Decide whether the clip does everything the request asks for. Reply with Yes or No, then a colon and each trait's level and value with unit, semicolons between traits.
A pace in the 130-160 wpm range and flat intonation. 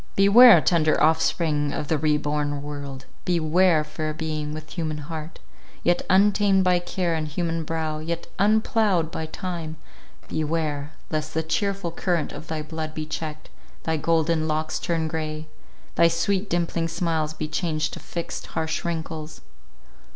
Yes: average, 145 wpm; narrow, 1.8 semitones